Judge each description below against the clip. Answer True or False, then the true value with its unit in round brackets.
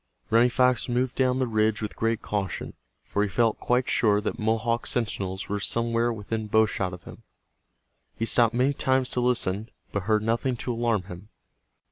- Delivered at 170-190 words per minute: True (180 wpm)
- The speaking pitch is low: True (115 Hz)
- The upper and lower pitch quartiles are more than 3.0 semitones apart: False (2.6 semitones)